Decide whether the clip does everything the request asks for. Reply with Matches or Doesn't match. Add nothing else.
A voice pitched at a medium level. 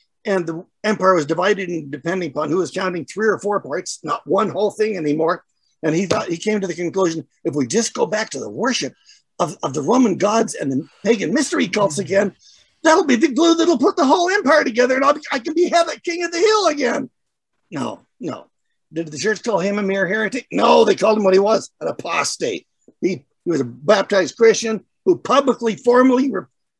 Doesn't match